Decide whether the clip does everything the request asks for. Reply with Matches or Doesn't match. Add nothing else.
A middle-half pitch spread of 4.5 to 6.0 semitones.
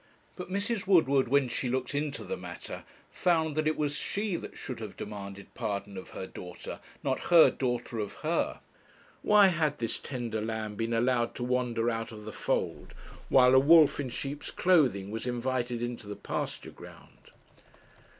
Matches